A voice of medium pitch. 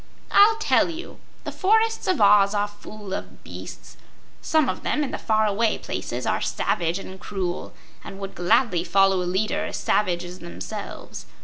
No: high, 205 Hz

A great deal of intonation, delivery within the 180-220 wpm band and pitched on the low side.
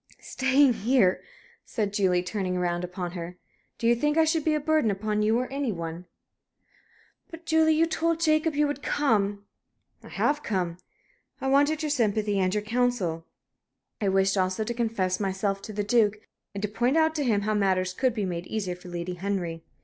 No: wide, 6.7 semitones; average, 190 wpm; high, 210 Hz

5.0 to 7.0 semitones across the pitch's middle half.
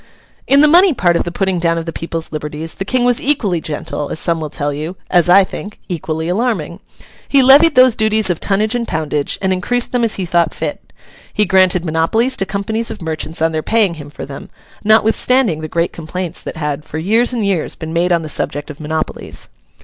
Yes: wide, 5.5 semitones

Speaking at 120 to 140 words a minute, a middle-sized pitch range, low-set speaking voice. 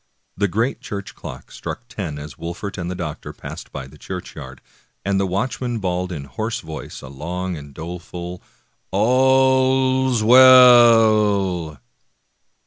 No: slow, 135 wpm; wide, 6.0 semitones; very low, 95 Hz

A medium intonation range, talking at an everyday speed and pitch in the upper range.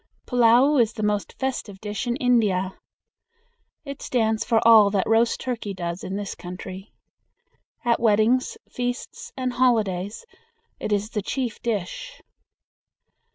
No: average, 3.5 semitones; slow, 130 wpm; high, 220 Hz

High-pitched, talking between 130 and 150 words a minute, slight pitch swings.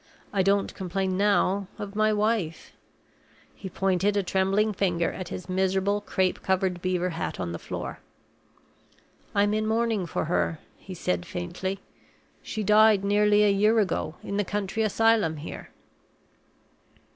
Yes: high, 195 Hz; average, 145 wpm; narrow, 2.1 semitones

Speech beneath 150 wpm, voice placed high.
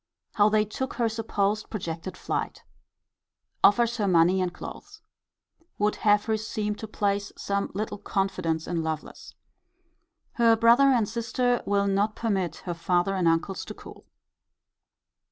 Yes: average, 140 wpm; high, 205 Hz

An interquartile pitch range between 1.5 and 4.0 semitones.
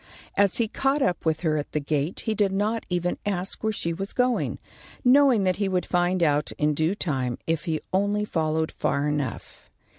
No: average, 4.8 semitones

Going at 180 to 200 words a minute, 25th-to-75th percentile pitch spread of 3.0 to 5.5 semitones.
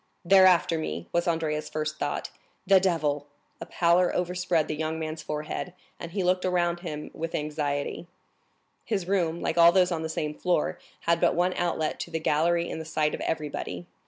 No: average, 185 wpm; narrow, 2.6 semitones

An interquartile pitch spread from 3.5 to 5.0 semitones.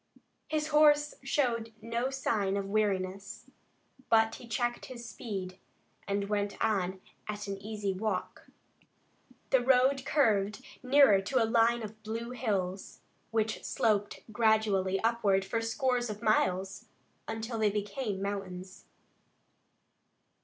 No: average, 3.1 semitones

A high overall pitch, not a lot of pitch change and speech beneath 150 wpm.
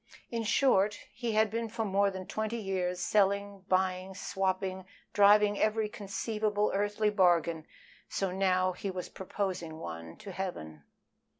Yes: high, 195 Hz; narrow, 2.2 semitones; slow, 135 wpm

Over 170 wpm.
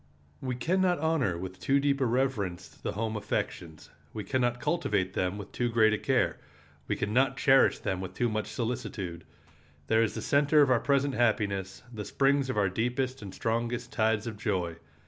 Yes: average, 195 wpm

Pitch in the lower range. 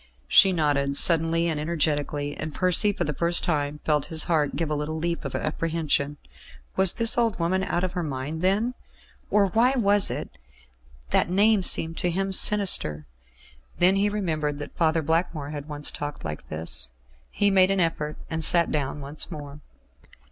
No: medium, 165 Hz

